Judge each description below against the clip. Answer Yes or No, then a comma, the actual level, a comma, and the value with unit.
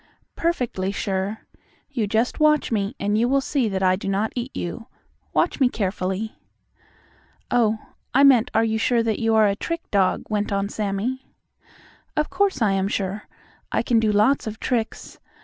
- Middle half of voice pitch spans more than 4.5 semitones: No, average, 3.7 semitones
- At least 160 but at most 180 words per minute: Yes, average, 175 wpm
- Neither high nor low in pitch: No, high, 220 Hz